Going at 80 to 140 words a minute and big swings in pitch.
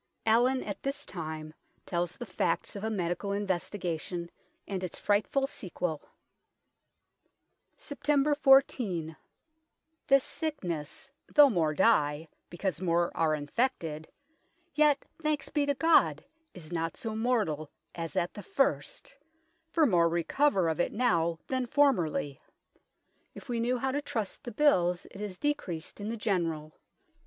Yes: slow, 135 wpm; wide, 8.1 semitones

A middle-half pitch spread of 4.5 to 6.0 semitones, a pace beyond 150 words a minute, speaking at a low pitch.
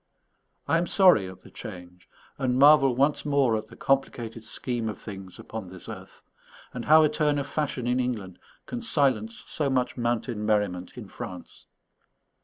Yes: average, 4.9 semitones; average, 170 wpm; low, 125 Hz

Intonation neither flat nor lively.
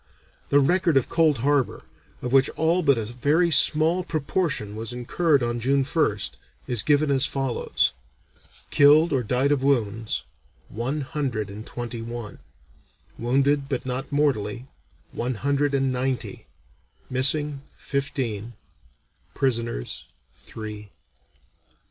Yes: average, 3.5 semitones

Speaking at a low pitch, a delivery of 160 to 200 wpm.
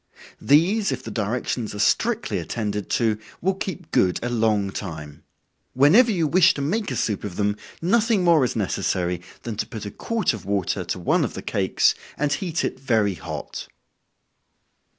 Yes: low, 115 Hz; average, 175 wpm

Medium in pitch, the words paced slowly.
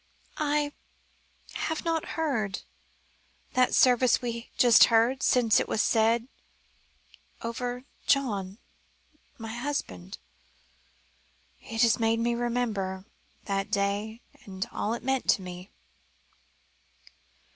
No: high, 230 Hz; slow, 105 wpm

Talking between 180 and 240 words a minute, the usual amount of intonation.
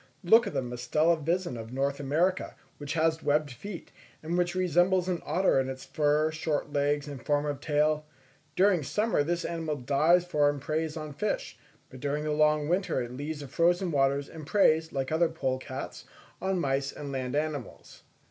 Yes: average, 185 wpm; average, 3.2 semitones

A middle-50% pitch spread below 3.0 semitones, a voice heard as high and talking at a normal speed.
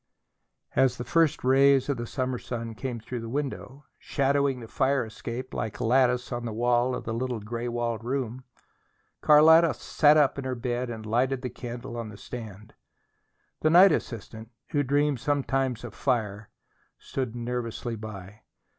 No: narrow, 2.6 semitones; low, 125 Hz; average, 165 wpm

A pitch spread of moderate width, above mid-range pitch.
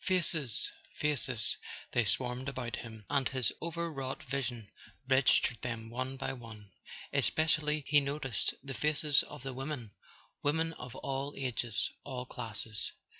No: average, 3.5 semitones; low, 130 Hz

